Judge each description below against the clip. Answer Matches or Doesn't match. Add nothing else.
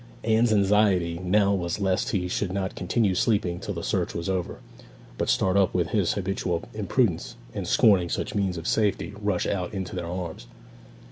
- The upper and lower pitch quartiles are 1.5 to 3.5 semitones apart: Matches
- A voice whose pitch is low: Matches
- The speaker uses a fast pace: Doesn't match